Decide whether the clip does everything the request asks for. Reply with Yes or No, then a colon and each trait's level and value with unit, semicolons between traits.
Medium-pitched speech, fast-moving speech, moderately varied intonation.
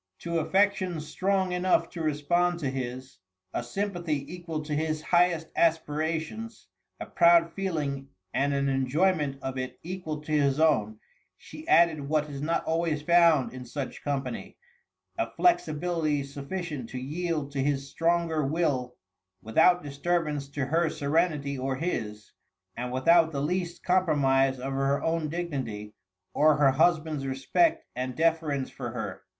No: medium, 155 Hz; average, 145 wpm; average, 3.8 semitones